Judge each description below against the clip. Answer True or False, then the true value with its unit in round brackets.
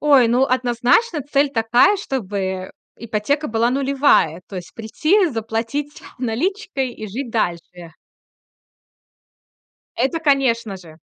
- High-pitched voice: True (245 Hz)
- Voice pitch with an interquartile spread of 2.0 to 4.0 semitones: False (4.6 semitones)